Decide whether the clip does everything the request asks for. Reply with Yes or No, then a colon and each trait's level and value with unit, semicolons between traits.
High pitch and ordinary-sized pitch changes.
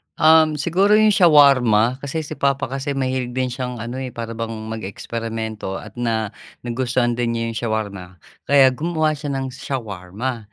No: low, 125 Hz; average, 3.8 semitones